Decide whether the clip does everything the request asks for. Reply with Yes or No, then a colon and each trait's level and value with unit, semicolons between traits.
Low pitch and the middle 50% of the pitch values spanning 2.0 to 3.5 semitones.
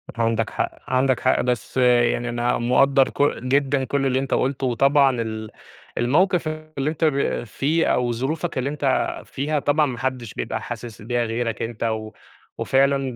Yes: low, 130 Hz; average, 2.7 semitones